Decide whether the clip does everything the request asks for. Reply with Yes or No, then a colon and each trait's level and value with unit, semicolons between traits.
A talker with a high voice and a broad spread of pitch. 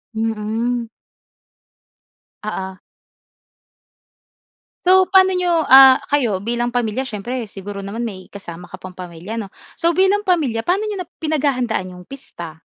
Yes: high, 235 Hz; wide, 7.3 semitones